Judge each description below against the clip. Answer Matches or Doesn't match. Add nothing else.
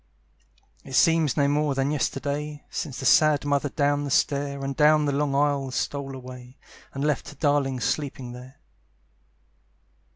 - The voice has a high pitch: Doesn't match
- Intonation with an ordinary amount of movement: Doesn't match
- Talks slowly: Doesn't match